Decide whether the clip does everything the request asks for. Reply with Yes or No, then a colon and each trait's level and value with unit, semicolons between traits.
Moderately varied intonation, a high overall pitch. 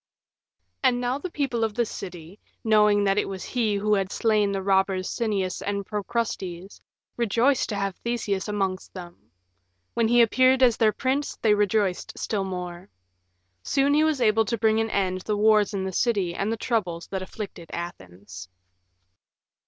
Yes: average, 3.5 semitones; high, 210 Hz